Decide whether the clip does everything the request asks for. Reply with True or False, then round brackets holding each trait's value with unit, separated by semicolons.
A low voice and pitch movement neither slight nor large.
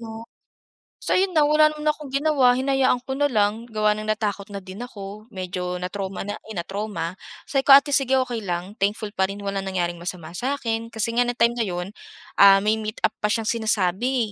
False (215 Hz; 4.1 semitones)